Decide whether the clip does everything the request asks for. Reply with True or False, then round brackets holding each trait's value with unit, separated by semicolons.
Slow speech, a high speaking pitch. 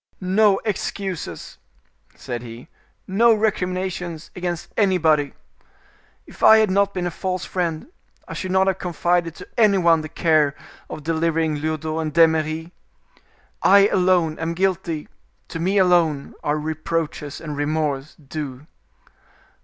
False (130 wpm; 165 Hz)